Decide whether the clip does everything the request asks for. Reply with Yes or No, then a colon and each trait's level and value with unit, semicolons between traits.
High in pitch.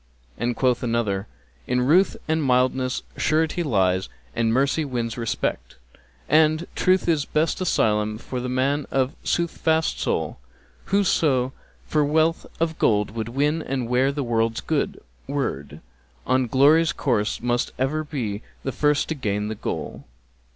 No: low, 130 Hz